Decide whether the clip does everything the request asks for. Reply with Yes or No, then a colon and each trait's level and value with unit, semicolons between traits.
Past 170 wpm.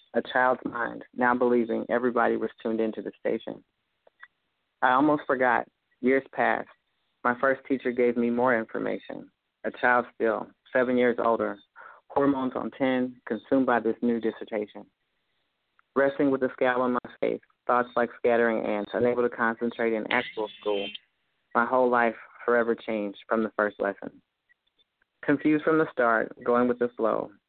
No: average, 155 wpm